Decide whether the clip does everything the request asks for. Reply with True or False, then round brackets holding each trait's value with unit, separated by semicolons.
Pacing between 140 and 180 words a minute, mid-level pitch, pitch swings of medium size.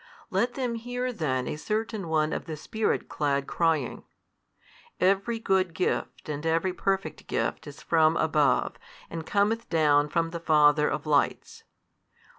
True (145 wpm; 165 Hz; 5.0 semitones)